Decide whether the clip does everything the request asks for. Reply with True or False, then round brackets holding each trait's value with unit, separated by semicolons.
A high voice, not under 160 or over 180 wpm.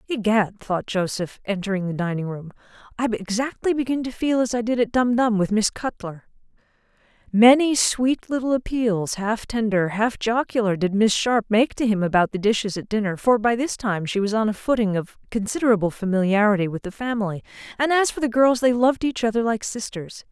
False (220 Hz; 190 wpm)